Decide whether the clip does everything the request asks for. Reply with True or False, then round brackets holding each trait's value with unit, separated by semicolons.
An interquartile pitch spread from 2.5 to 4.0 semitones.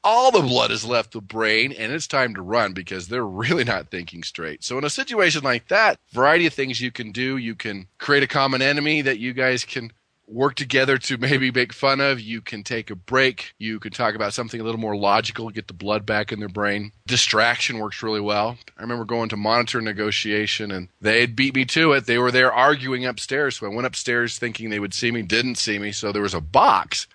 True (3.6 semitones)